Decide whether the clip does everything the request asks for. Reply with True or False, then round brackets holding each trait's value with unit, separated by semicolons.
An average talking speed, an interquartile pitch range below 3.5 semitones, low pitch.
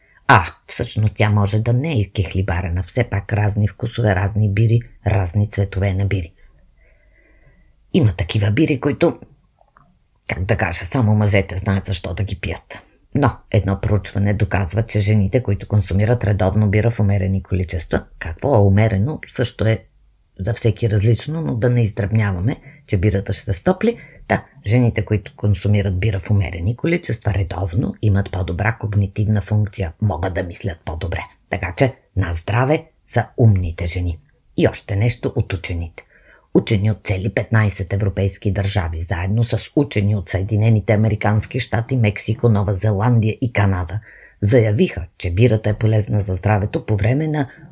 True (150 wpm; 2.7 semitones; 105 Hz)